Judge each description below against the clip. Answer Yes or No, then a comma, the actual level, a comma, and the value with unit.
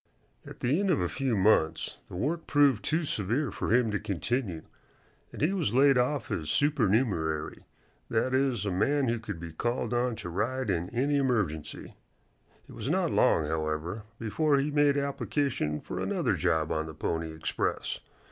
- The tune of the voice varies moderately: No, wide, 8.2 semitones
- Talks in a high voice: No, low, 120 Hz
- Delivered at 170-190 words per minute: Yes, average, 175 wpm